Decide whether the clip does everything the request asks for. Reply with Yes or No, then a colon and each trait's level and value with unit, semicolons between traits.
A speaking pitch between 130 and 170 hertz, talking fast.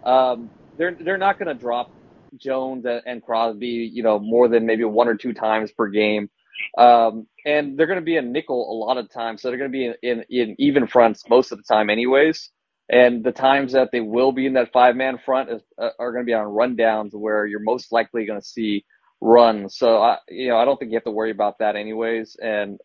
No: low, 120 Hz; fast, 240 wpm